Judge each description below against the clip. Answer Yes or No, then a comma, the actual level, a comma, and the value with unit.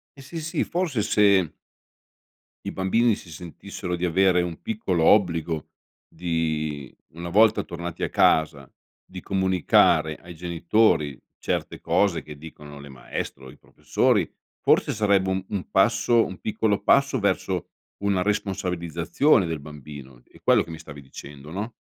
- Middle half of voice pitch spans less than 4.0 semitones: No, average, 4.5 semitones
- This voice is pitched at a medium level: No, very low, 90 Hz